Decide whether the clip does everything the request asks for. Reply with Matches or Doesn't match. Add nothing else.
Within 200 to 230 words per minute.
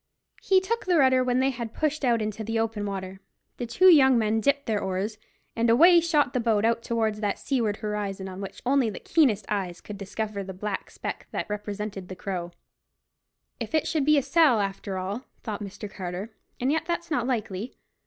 Matches